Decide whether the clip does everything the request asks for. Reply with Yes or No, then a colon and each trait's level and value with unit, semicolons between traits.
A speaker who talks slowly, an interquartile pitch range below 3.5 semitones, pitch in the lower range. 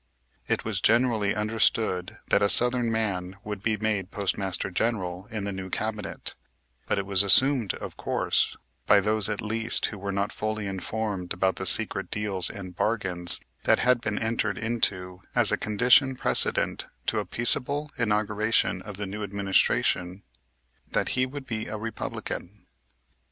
No: average, 155 wpm; narrow, 2.6 semitones; low, 105 Hz